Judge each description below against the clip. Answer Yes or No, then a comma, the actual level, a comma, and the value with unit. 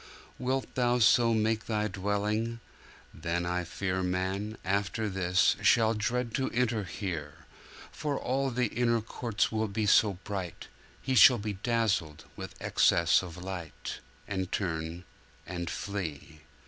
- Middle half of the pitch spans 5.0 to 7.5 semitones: No, average, 4.1 semitones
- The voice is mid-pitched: No, low, 105 Hz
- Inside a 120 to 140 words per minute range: Yes, slow, 135 wpm